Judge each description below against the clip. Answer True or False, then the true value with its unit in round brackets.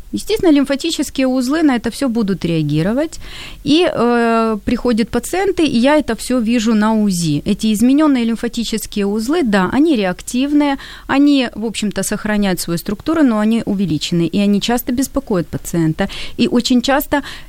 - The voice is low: False (235 Hz)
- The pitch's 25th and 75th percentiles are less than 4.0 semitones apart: False (5.2 semitones)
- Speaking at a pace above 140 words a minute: True (150 wpm)